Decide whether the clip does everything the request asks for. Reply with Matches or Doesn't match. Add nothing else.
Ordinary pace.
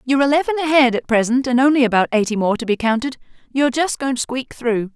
Doesn't match